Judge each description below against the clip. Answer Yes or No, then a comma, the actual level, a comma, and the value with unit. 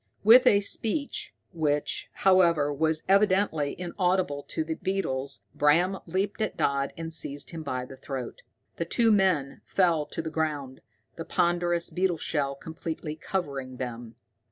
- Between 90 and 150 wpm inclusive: Yes, average, 145 wpm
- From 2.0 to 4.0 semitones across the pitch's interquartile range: No, average, 4.8 semitones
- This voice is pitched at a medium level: Yes, medium, 160 Hz